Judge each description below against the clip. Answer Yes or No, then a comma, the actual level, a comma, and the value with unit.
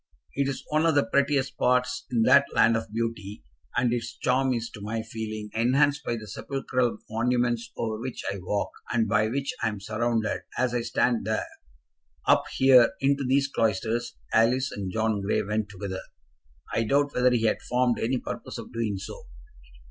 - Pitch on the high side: No, low, 115 Hz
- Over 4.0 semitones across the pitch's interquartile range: No, average, 2.8 semitones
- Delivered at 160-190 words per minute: Yes, average, 180 wpm